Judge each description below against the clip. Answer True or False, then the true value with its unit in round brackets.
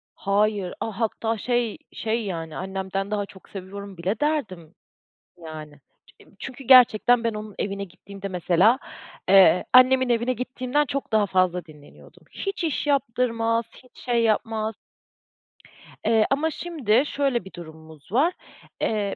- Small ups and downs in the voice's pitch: False (4.7 semitones)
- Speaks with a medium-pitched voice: False (215 Hz)